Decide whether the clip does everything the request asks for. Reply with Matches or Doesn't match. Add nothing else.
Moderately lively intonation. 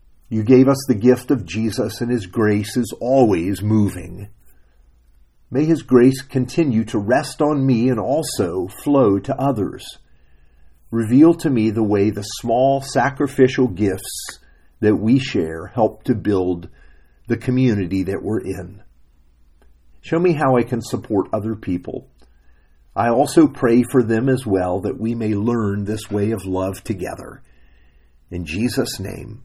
Doesn't match